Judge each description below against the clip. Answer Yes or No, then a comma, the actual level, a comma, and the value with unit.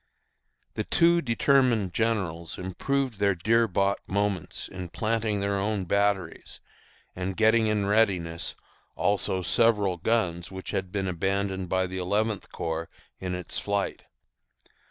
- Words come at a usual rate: No, slow, 130 wpm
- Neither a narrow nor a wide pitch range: Yes, average, 3.1 semitones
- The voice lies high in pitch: No, low, 100 Hz